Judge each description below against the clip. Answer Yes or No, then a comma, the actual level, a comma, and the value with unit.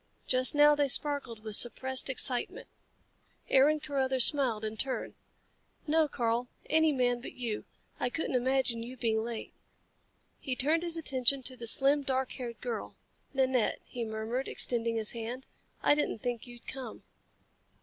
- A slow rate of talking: No, average, 150 wpm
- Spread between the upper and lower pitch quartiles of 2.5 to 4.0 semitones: Yes, average, 2.8 semitones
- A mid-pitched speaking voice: No, very high, 255 Hz